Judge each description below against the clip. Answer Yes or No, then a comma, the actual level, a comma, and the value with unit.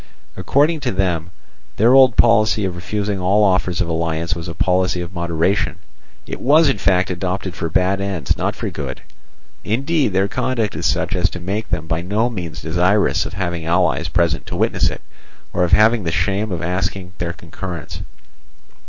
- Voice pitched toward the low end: Yes, very low, 95 Hz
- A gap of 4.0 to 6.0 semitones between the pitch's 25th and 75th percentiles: No, average, 3.5 semitones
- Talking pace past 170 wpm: Yes, average, 180 wpm